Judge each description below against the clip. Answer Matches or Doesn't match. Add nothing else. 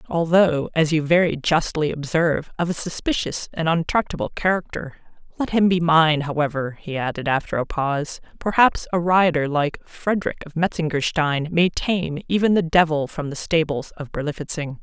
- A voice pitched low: Doesn't match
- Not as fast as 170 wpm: Matches